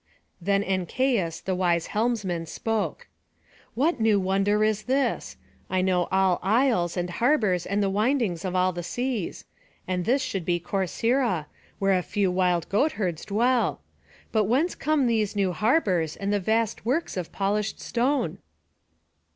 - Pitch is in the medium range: No, high, 200 Hz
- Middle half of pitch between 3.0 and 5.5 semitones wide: Yes, average, 4.3 semitones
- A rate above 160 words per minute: No, average, 145 wpm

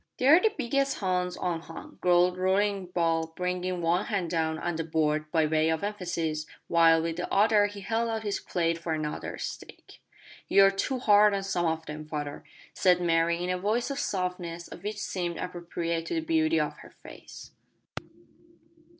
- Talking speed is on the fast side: No, average, 175 wpm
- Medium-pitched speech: Yes, medium, 180 Hz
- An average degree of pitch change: Yes, average, 3.7 semitones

